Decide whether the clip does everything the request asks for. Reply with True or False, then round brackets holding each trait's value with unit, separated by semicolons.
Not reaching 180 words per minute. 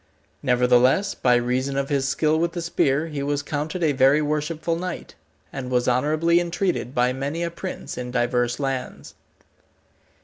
True (160 wpm)